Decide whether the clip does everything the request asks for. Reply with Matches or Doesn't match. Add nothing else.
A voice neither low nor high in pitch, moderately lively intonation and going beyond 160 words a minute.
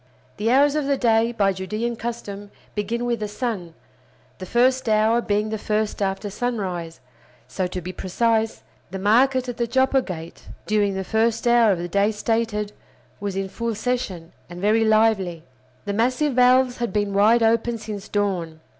Doesn't match